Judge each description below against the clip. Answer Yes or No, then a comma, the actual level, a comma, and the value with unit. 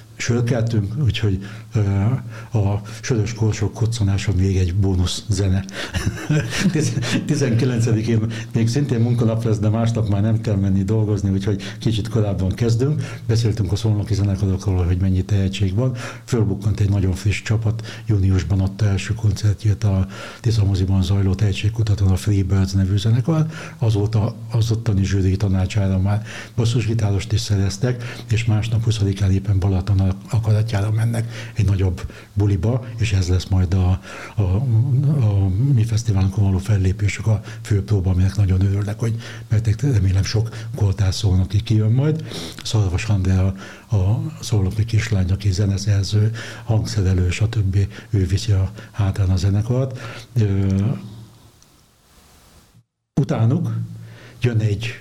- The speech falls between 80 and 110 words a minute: No, average, 130 wpm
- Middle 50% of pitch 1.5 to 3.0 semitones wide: Yes, narrow, 2.6 semitones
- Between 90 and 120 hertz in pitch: Yes, low, 105 Hz